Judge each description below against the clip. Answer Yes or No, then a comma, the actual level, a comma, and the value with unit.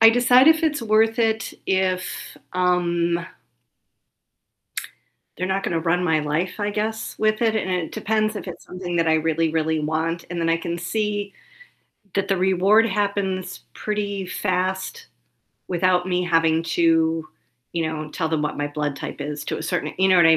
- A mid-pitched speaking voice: Yes, medium, 180 Hz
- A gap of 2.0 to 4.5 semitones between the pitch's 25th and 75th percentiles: Yes, average, 3.9 semitones